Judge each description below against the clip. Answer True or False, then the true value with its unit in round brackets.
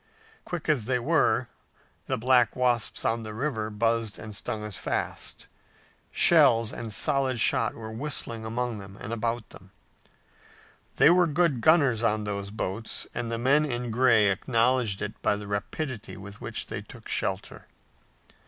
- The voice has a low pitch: True (115 Hz)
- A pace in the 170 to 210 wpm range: False (160 wpm)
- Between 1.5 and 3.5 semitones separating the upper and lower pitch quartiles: True (3.1 semitones)